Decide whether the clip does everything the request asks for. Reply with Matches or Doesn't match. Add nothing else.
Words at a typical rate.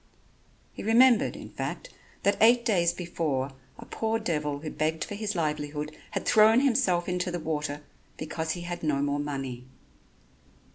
Matches